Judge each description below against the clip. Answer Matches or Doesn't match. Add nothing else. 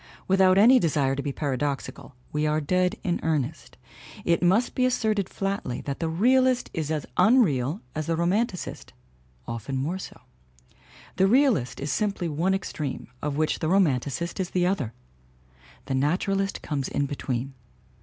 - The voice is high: Doesn't match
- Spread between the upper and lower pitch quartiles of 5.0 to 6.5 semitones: Matches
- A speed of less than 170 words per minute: Matches